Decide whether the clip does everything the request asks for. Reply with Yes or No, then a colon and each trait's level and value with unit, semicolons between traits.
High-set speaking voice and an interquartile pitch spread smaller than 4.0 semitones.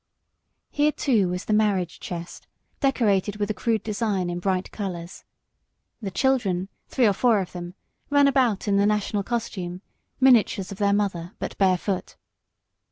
Yes: high, 200 Hz; average, 3.5 semitones